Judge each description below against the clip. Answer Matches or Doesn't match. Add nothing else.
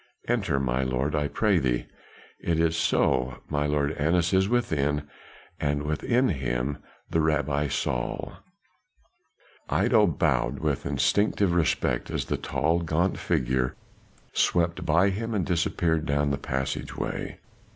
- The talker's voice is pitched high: Doesn't match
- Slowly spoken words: Matches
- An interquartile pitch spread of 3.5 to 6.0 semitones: Matches